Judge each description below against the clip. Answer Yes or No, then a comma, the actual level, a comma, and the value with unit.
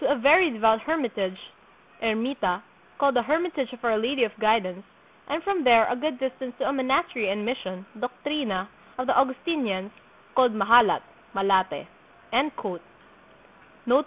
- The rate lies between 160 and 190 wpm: No, slow, 135 wpm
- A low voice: No, high, 245 Hz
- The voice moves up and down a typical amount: Yes, average, 4.4 semitones